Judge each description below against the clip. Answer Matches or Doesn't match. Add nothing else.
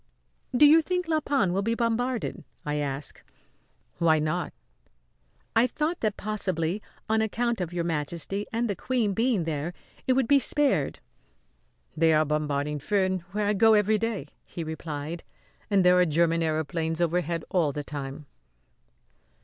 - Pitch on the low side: Doesn't match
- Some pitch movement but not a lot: Doesn't match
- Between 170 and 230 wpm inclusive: Doesn't match